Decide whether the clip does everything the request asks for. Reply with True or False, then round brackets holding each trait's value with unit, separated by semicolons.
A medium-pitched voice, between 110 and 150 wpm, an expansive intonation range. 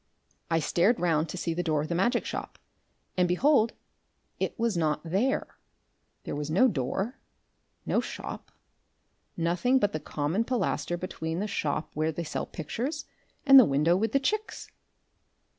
False (180 Hz; 160 wpm; 6.5 semitones)